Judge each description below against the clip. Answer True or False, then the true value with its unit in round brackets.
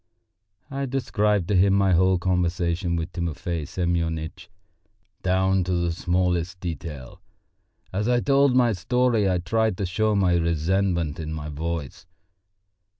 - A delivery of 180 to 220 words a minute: False (135 wpm)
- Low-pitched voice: True (90 Hz)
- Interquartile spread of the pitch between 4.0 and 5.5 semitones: False (2.9 semitones)